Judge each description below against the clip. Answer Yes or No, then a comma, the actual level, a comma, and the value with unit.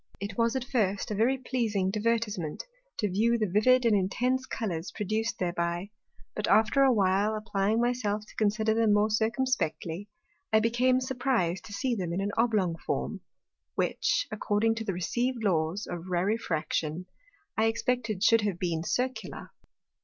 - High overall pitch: Yes, high, 215 Hz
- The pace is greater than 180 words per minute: No, average, 160 wpm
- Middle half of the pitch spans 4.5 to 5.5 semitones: No, average, 3.5 semitones